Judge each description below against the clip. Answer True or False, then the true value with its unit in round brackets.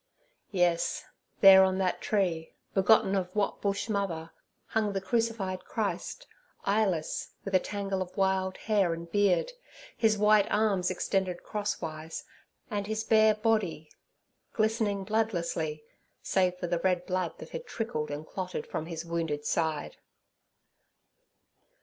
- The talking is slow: True (125 wpm)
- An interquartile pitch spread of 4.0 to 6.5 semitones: False (3.5 semitones)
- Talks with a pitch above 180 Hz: True (190 Hz)